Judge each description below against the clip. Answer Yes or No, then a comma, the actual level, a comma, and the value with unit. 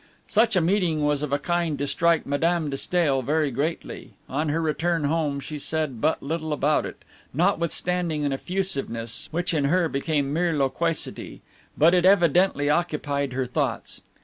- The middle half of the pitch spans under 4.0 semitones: Yes, average, 3.3 semitones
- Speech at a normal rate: Yes, average, 165 wpm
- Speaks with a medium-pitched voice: Yes, medium, 155 Hz